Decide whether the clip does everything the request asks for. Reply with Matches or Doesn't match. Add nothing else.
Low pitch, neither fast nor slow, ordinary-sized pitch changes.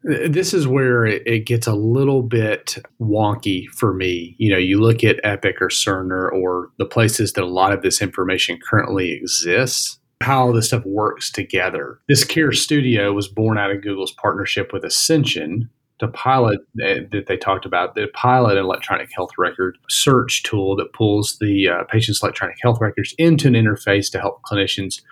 Matches